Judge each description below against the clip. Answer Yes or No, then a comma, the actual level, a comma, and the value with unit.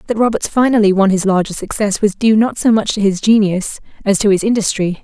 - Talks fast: Yes, fast, 225 wpm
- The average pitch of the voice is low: No, high, 205 Hz